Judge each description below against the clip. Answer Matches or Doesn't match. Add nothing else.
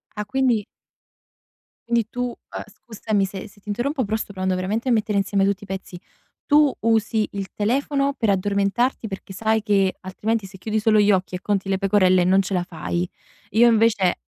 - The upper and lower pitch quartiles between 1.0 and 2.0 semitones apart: Doesn't match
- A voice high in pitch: Matches